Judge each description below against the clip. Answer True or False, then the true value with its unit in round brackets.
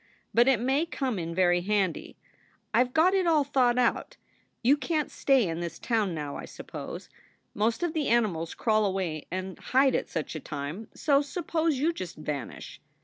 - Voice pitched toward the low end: False (230 Hz)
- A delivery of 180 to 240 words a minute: True (190 wpm)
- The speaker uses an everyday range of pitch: False (7.9 semitones)